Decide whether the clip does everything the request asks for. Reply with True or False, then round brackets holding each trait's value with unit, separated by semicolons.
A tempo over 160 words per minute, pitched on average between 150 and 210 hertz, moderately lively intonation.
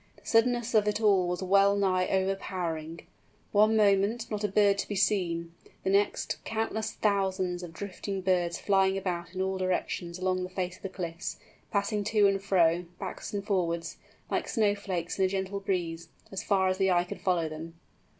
False (185 wpm; 190 Hz; 2.2 semitones)